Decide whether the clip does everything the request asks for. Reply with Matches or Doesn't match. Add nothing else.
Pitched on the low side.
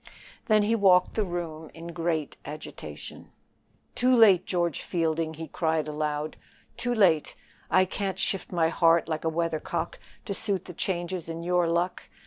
Doesn't match